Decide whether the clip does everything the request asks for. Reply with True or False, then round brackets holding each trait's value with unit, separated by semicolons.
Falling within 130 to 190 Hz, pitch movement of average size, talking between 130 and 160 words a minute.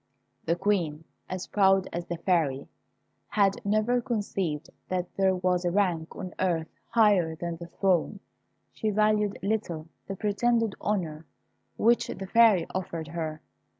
True (185 Hz; 3.7 semitones; 140 wpm)